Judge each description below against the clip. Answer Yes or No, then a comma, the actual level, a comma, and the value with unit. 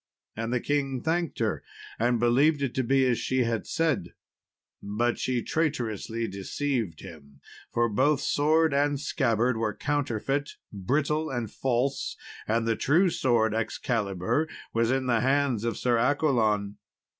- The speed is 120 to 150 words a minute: Yes, average, 140 wpm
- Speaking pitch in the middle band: No, low, 125 Hz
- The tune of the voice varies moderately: Yes, average, 4.1 semitones